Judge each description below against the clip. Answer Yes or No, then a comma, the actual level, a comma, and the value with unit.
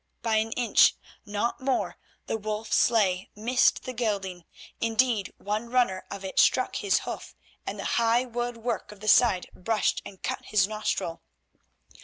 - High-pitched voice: Yes, high, 220 Hz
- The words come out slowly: No, average, 150 wpm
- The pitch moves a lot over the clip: No, average, 2.9 semitones